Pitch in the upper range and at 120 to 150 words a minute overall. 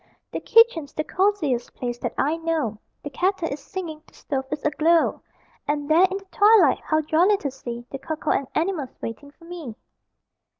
No: very high, 310 Hz; average, 180 wpm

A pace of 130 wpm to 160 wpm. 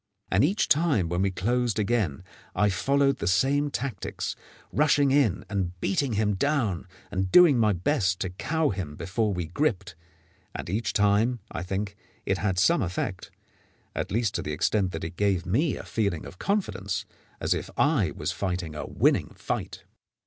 No: average, 170 wpm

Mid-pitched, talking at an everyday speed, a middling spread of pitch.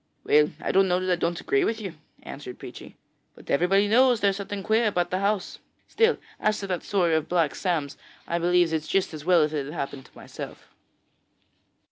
No: medium, 180 Hz; fast, 215 wpm; average, 4.0 semitones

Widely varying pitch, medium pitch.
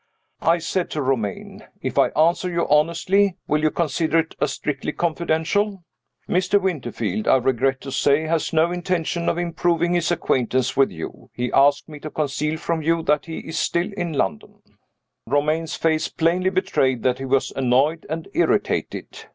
No: average, 3.9 semitones; medium, 160 Hz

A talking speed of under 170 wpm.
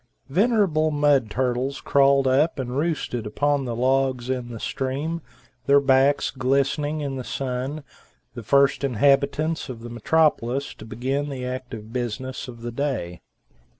Yes: average, 150 wpm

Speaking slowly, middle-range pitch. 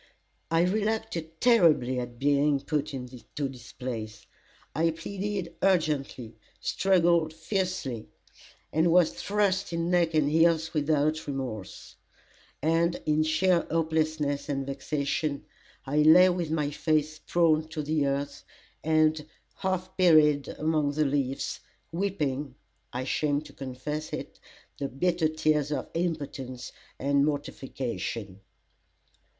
Yes: slow, 115 wpm; medium, 155 Hz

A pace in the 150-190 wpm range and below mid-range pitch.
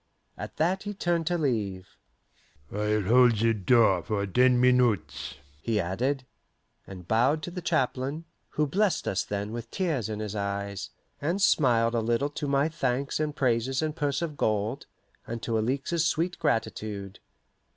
Yes: average, 160 wpm; low, 120 Hz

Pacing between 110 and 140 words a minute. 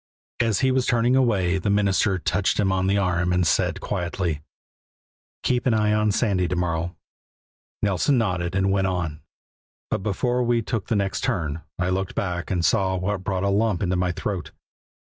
No: average, 185 wpm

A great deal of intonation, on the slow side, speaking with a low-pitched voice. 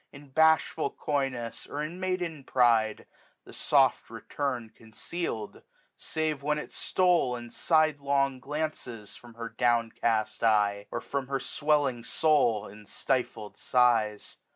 No: average, 4.7 semitones; slow, 130 wpm; low, 130 Hz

